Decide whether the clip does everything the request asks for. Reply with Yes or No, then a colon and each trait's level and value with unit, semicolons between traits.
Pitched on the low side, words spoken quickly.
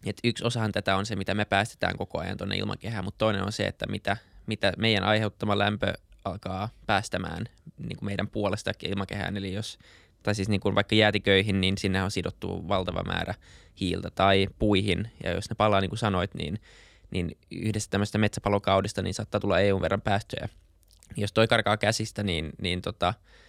Yes: low, 100 Hz; fast, 180 wpm